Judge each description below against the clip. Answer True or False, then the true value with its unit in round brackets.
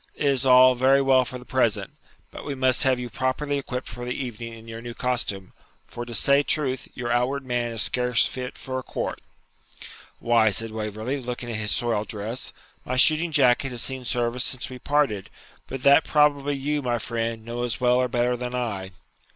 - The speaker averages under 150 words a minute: False (200 wpm)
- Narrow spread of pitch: True (2.1 semitones)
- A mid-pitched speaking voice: False (125 Hz)